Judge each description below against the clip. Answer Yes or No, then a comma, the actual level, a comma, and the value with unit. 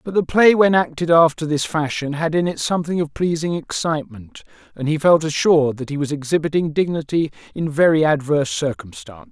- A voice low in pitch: No, medium, 155 Hz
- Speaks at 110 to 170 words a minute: No, average, 180 wpm